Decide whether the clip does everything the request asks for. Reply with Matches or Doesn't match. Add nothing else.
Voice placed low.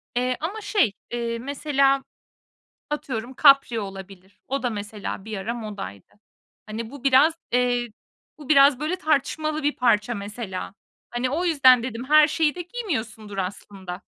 Doesn't match